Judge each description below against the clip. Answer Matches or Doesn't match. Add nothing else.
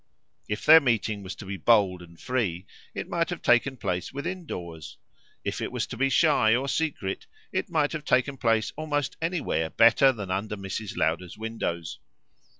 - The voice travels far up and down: Matches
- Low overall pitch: Matches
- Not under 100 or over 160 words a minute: Doesn't match